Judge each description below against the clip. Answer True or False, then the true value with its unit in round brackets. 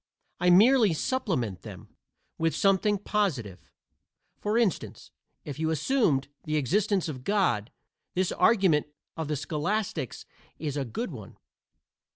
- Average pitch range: False (6.3 semitones)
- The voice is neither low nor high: True (165 Hz)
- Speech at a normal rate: False (125 wpm)